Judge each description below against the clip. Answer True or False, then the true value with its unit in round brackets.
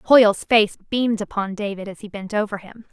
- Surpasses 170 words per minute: True (205 wpm)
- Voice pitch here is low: False (210 Hz)